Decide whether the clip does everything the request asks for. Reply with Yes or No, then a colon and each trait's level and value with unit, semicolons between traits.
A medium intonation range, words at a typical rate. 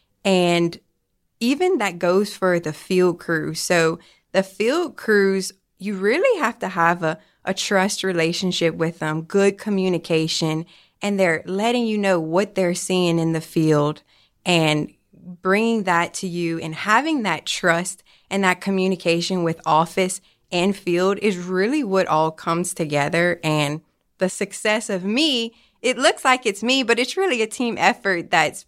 Yes: average, 3.4 semitones; average, 155 wpm